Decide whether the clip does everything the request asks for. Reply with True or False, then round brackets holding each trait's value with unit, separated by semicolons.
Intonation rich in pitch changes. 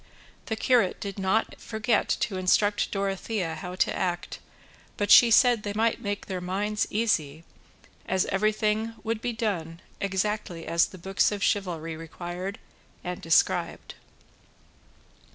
False (3.2 semitones)